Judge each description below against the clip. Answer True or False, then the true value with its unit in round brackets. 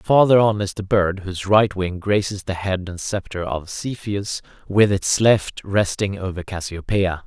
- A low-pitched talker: True (100 Hz)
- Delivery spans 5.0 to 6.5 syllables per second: False (4.3 syllables/s)